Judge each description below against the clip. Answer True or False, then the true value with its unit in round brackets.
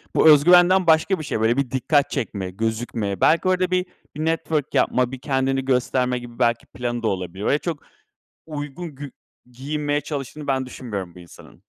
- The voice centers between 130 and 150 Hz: True (135 Hz)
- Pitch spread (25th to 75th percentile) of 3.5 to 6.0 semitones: True (4.4 semitones)